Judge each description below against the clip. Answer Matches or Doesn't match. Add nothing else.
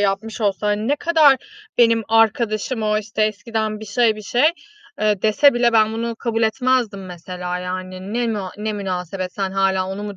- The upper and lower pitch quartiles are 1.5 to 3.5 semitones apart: Matches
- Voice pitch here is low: Doesn't match